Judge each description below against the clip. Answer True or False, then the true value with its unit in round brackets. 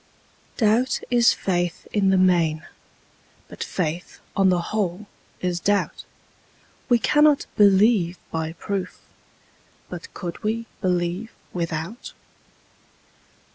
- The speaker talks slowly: True (100 wpm)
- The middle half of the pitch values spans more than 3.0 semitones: True (3.7 semitones)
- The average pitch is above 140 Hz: True (185 Hz)